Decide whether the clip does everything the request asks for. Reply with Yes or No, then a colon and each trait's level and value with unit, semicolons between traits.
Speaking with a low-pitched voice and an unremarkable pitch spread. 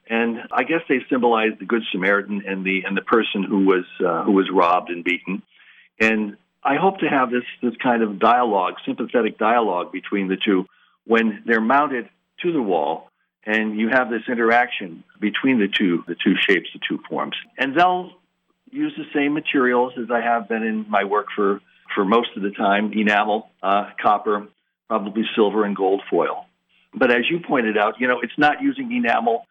Yes: low, 110 Hz; average, 3.7 semitones